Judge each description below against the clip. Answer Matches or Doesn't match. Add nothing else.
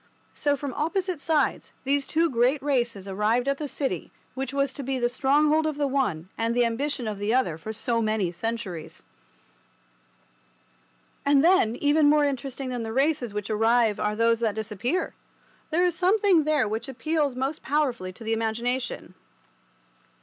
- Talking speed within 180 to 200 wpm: Doesn't match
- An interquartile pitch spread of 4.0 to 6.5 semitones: Matches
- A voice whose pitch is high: Matches